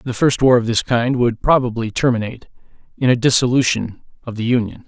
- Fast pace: No, average, 185 wpm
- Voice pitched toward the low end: Yes, low, 120 Hz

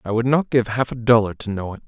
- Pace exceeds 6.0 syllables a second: Yes, 6.3 syllables/s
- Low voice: Yes, low, 115 Hz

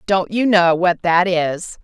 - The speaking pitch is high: No, medium, 180 Hz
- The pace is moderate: Yes, average, 195 wpm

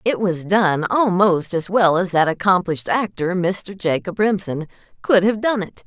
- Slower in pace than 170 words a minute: No, average, 175 wpm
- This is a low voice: No, high, 190 Hz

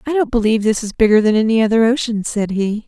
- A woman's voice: Yes, female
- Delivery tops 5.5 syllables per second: Yes, 6.3 syllables/s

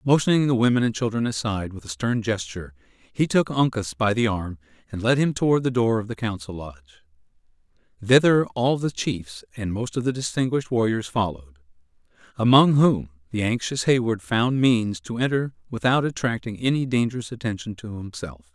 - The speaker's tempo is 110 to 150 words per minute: No, average, 170 wpm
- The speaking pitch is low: Yes, low, 110 Hz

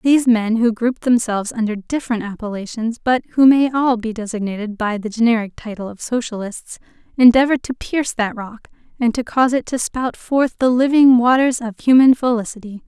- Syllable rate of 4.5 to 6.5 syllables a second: Yes, 5.7 syllables/s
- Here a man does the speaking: No, female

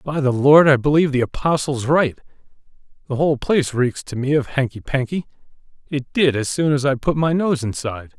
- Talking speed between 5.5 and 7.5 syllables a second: Yes, 5.9 syllables/s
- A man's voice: Yes, male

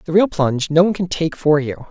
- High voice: No, medium, 160 Hz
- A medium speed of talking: No, fast, 285 wpm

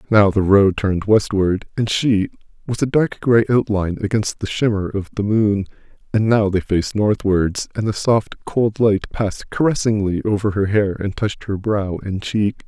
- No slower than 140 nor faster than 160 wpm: No, average, 185 wpm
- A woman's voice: No, male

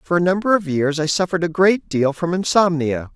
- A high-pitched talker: No, medium, 170 Hz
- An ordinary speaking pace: No, fast, 230 wpm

